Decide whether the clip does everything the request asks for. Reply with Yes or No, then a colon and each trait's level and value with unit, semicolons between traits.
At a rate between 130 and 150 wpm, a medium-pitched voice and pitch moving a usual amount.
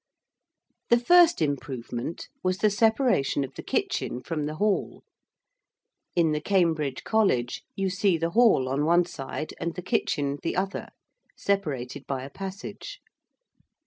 No: average, 140 wpm; medium, 170 Hz; wide, 6.0 semitones